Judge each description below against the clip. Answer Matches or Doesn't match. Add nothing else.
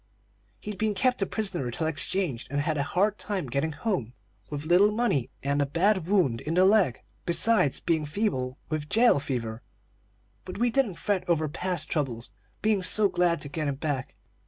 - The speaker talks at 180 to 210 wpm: Matches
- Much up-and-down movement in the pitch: Matches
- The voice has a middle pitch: Matches